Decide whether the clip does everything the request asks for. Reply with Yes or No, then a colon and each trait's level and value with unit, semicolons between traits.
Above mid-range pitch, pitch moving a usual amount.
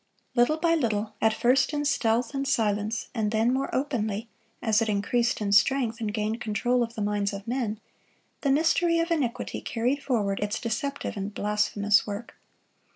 Yes: high, 225 Hz; average, 3.9 semitones